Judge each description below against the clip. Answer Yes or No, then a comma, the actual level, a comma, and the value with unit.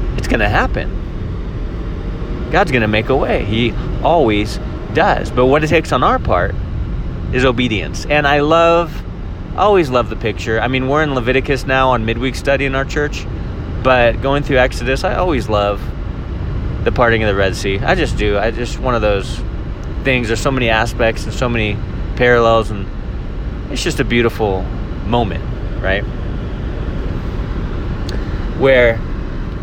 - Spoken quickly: No, average, 160 wpm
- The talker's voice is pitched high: No, low, 115 Hz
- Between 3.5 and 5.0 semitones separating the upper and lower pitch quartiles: Yes, average, 4.1 semitones